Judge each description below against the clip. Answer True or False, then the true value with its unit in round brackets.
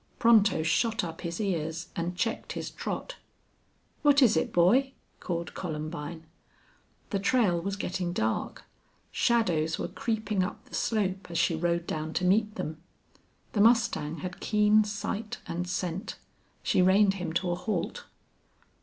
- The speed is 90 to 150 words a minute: True (145 wpm)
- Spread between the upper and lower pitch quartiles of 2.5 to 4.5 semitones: True (4.1 semitones)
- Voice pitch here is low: False (185 Hz)